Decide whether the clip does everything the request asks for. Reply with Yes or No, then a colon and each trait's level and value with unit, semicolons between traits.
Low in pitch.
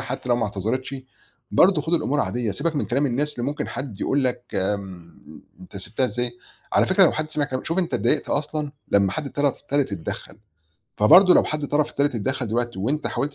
Yes: low, 130 Hz